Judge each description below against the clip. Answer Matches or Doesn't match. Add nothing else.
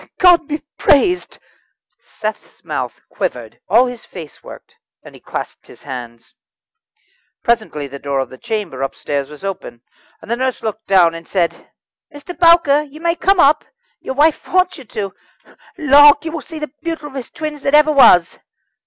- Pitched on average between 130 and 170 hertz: Doesn't match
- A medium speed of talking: Matches